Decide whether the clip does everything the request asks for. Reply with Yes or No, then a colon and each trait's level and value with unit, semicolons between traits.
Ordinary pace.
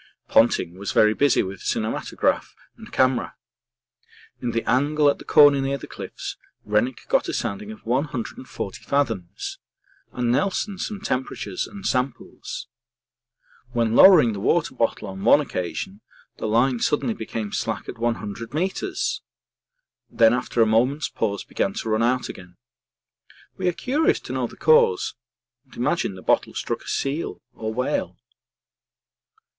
Yes: average, 145 wpm